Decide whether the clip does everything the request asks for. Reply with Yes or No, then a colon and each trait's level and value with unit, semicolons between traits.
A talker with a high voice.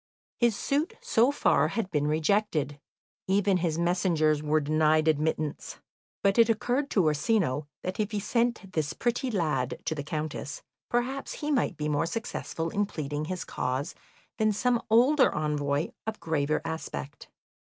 No: medium, 170 Hz